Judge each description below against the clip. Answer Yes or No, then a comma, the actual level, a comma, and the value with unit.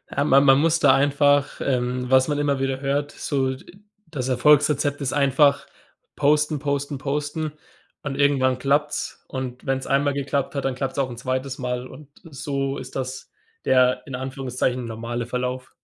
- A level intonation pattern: Yes, narrow, 1.8 semitones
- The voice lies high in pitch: No, low, 135 Hz